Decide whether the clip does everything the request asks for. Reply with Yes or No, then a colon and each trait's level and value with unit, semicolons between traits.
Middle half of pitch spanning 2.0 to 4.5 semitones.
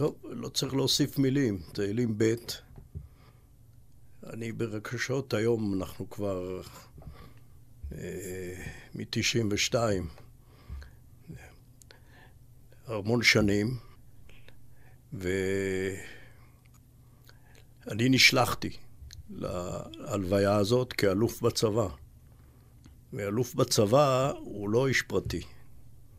Yes: average, 3.3 semitones